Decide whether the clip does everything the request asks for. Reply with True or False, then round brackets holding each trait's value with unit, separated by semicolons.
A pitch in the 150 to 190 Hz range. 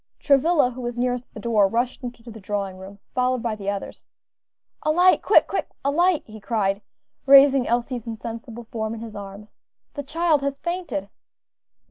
False (240 Hz)